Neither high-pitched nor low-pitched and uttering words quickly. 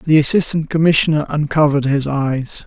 No: medium, 150 Hz; slow, 135 wpm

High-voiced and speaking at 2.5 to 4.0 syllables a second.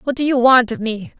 No: high, 245 Hz; 5.3 syllables/s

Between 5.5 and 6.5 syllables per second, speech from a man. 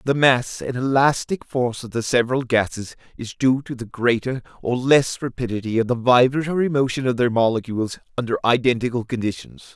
Yes: 5.6 syllables/s; male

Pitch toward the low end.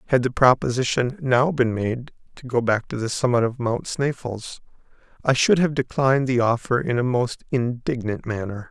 Yes: low, 125 Hz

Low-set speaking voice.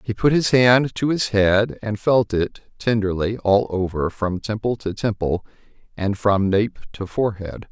Yes: low, 105 Hz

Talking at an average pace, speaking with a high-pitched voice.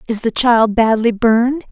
Yes: average, 175 wpm; high, 230 Hz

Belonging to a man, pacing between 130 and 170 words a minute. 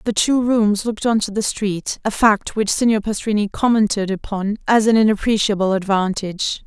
No: female; average, 155 wpm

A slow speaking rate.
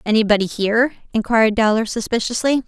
Yes: slow, 110 wpm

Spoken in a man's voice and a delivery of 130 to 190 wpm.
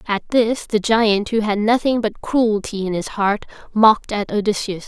No: female; average, 185 wpm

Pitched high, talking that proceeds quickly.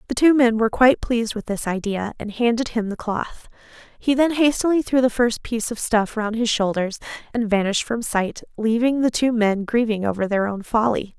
Yes: high, 225 Hz; fast, 210 wpm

